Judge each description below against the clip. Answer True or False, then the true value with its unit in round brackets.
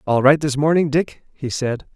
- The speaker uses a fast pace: True (215 wpm)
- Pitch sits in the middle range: True (145 Hz)